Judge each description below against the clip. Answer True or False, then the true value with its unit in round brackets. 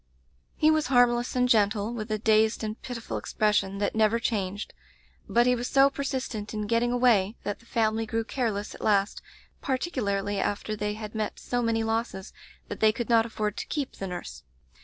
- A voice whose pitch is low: False (220 Hz)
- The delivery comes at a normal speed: True (185 wpm)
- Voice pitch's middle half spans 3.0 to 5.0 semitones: False (2.6 semitones)